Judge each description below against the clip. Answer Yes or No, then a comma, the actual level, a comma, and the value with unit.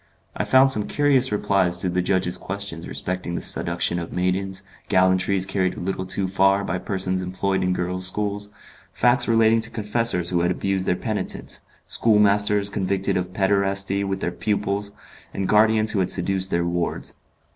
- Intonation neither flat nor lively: No, narrow, 2.0 semitones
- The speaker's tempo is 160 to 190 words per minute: Yes, average, 165 wpm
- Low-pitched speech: Yes, very low, 95 Hz